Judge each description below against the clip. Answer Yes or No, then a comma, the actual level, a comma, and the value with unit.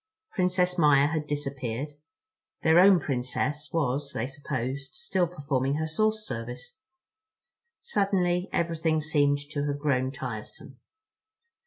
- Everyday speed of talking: No, slow, 115 wpm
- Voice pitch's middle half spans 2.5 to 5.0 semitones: Yes, average, 4.0 semitones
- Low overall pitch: No, medium, 150 Hz